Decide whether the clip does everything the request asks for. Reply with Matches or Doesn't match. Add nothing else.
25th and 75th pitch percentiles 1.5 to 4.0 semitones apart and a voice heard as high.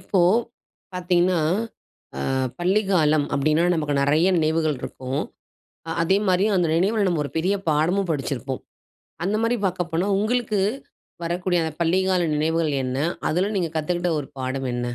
Doesn't match